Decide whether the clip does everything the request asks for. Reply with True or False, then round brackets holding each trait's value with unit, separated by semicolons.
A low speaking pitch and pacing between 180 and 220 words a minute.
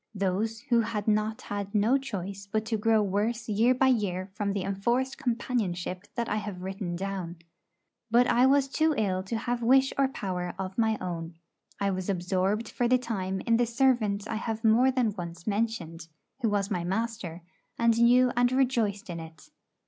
False (215 Hz; 185 wpm)